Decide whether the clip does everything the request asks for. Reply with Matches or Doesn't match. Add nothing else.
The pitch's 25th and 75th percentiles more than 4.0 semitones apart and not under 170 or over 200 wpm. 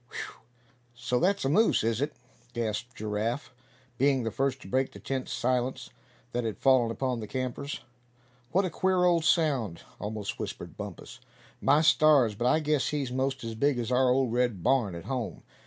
Doesn't match